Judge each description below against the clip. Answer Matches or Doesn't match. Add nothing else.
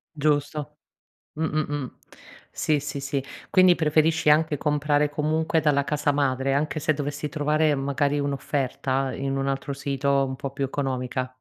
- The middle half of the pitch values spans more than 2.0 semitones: Doesn't match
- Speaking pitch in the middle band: Matches